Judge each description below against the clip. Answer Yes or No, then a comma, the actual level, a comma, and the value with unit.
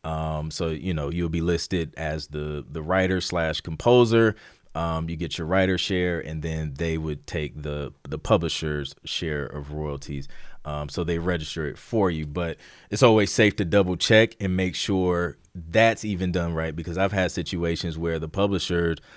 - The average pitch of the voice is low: Yes, very low, 85 Hz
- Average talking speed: Yes, average, 180 wpm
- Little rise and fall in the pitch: No, average, 3.1 semitones